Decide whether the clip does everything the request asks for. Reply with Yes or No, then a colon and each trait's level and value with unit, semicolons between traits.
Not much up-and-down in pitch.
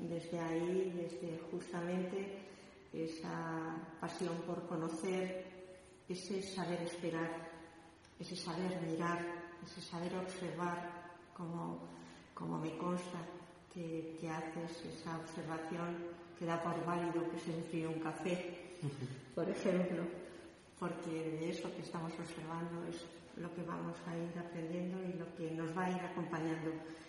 Yes: narrow, 1.2 semitones